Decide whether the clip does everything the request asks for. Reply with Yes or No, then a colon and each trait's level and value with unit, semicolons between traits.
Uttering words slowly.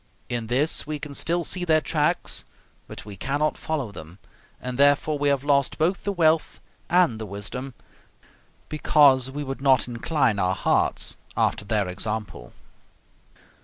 No: average, 150 wpm